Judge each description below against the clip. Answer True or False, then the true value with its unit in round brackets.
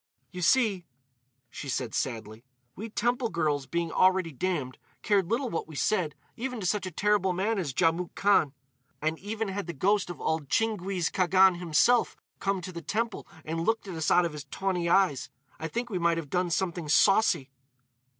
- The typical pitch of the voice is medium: True (180 Hz)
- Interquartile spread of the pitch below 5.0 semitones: True (4.0 semitones)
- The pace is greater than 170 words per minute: True (185 wpm)